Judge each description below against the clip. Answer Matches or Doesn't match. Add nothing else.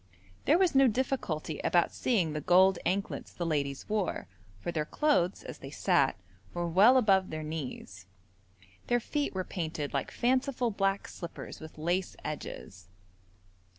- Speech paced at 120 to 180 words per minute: Matches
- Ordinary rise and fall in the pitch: Doesn't match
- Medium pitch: Matches